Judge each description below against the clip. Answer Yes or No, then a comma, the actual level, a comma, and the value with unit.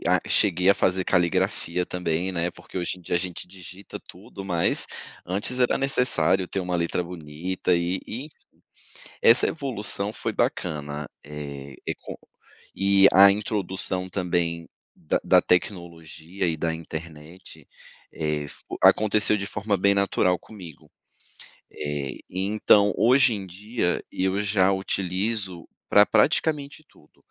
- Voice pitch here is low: Yes, very low, 95 Hz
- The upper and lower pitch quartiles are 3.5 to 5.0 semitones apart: No, average, 3.1 semitones